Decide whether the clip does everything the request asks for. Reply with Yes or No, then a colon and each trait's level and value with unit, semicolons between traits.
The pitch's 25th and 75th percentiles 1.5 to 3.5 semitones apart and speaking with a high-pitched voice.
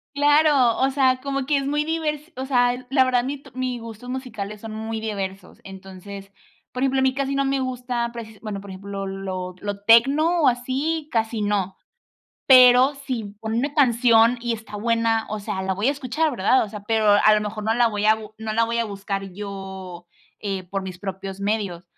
No: average, 4.5 semitones; high, 225 Hz